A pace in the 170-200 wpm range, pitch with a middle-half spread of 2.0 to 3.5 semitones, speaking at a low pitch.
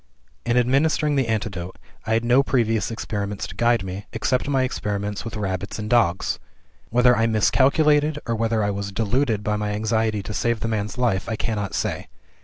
Yes: average, 185 wpm; average, 3.0 semitones; low, 110 Hz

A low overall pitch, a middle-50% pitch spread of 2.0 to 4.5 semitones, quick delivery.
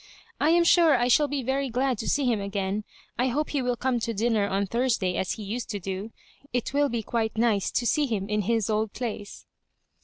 No: high, 235 Hz; average, 3.9 semitones; fast, 225 wpm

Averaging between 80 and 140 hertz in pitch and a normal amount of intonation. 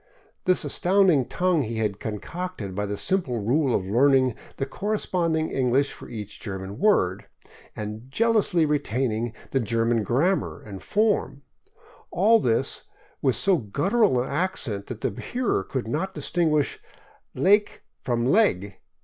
No: low, 135 Hz; wide, 8.8 semitones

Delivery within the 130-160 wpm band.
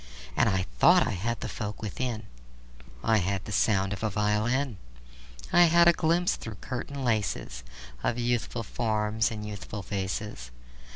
Yes: average, 155 wpm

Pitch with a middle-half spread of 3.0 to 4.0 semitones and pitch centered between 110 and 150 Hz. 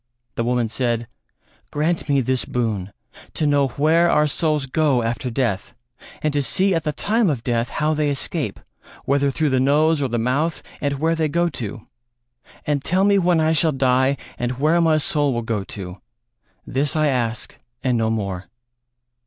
No: average, 4.4 semitones; medium, 140 Hz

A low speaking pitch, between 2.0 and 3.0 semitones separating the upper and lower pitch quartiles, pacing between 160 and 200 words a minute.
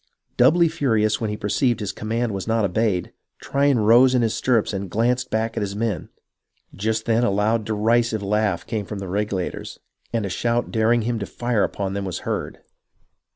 Yes: low, 110 Hz; narrow, 2.5 semitones; average, 195 wpm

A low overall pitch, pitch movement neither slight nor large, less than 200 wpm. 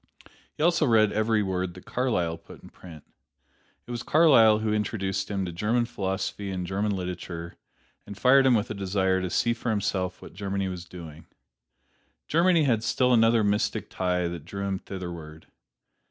Yes: low, 100 Hz; average, 3.7 semitones; average, 170 wpm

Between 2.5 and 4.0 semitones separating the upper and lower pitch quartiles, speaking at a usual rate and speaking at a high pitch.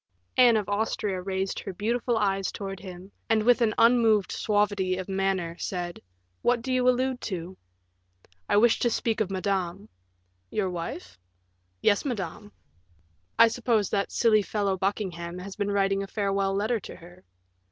Yes: average, 2.9 semitones; average, 155 wpm; high, 200 Hz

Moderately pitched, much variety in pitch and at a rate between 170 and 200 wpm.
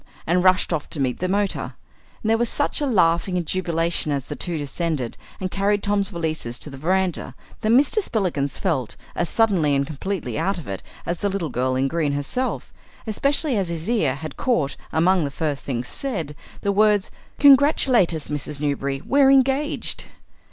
Yes: medium, 175 Hz; wide, 6.0 semitones; average, 185 wpm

